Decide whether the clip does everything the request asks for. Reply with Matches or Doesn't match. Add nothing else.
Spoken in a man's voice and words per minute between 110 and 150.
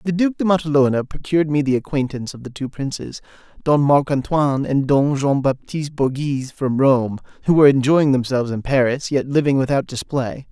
Doesn't match